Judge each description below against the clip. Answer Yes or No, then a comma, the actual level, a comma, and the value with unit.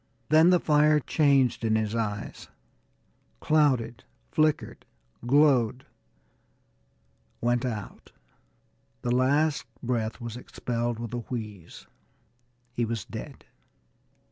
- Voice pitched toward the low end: Yes, low, 120 Hz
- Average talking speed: No, slow, 95 wpm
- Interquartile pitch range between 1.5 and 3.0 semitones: No, average, 4.2 semitones